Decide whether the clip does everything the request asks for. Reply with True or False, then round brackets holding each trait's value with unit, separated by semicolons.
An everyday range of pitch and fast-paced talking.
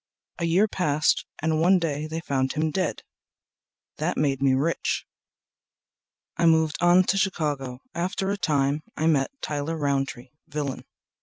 False (3.2 semitones; 140 wpm)